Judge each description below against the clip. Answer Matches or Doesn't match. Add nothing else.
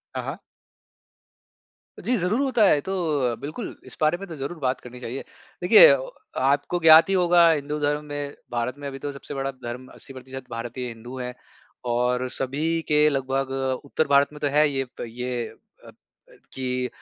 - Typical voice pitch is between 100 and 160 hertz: Matches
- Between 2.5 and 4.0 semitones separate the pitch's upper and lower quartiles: Matches